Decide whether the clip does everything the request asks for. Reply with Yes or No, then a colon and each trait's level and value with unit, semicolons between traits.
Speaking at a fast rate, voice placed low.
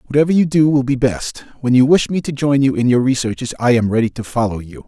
Yes: fast, 270 wpm; low, 130 Hz